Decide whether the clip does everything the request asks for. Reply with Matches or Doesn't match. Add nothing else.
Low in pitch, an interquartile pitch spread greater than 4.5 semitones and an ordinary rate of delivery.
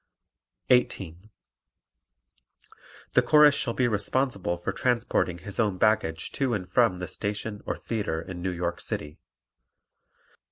Doesn't match